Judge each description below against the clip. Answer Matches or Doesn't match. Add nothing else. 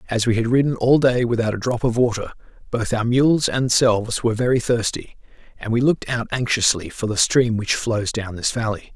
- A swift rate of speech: Matches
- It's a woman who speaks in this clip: Doesn't match